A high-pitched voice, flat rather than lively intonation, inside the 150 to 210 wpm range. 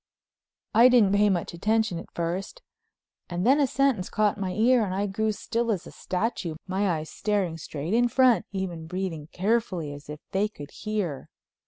No: high, 195 Hz; average, 4.3 semitones; average, 180 wpm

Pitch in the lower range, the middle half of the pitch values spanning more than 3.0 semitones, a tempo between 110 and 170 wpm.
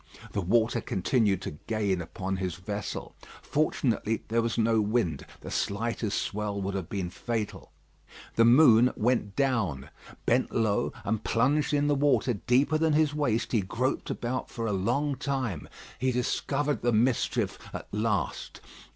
Yes: low, 115 Hz; average, 4.1 semitones; average, 150 wpm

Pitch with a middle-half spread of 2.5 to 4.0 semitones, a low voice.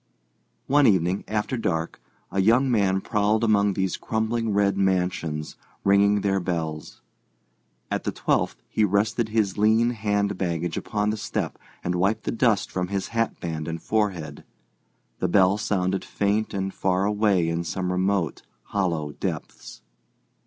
Yes: average, 2.8 semitones; low, 100 Hz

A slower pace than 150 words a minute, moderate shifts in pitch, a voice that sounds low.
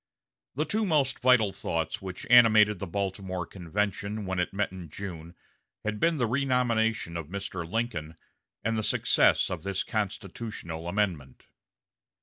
Yes: average, 140 wpm; average, 4.2 semitones; low, 100 Hz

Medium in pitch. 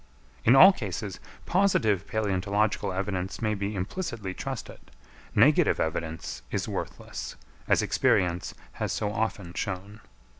No: low, 100 Hz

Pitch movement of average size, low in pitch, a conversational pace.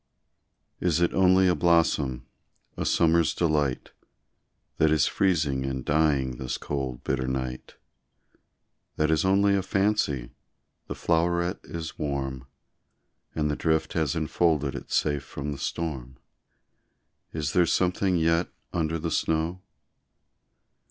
No: average, 3.9 semitones; very low, 80 Hz; slow, 125 wpm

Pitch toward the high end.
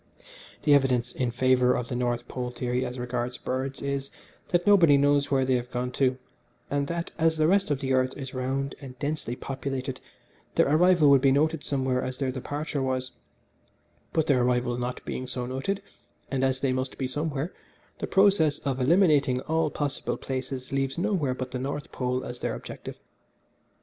No: low, 135 Hz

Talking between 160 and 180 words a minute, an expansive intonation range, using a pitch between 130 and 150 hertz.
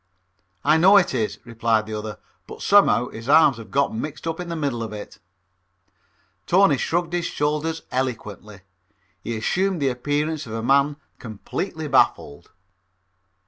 No: average, 150 wpm; wide, 6.1 semitones; medium, 140 Hz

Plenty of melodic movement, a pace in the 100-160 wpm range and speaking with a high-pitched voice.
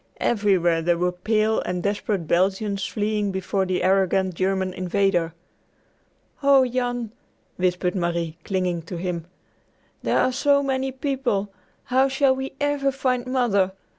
Yes: wide, 5.8 semitones; slow, 135 wpm; high, 200 Hz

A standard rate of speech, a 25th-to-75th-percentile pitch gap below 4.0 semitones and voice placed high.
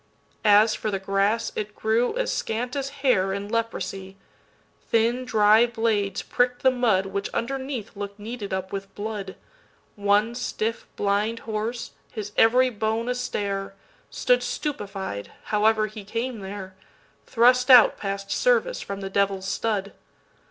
No: slow, 125 wpm; average, 3.3 semitones; high, 215 Hz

